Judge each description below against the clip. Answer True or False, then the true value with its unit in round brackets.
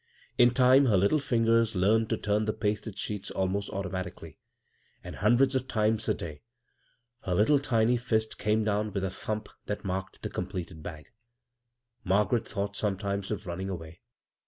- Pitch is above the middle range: False (105 Hz)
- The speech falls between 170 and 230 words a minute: False (160 wpm)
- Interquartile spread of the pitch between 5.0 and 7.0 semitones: False (2.9 semitones)